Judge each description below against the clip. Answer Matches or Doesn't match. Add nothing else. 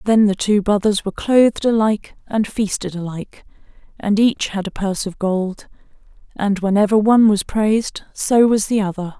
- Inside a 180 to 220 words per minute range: Doesn't match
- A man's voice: Doesn't match